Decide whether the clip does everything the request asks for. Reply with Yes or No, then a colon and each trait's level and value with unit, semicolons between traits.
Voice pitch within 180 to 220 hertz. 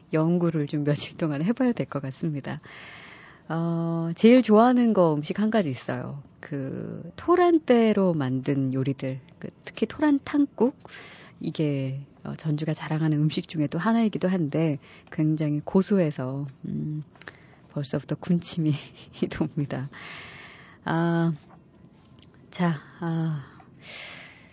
No: medium, 160 Hz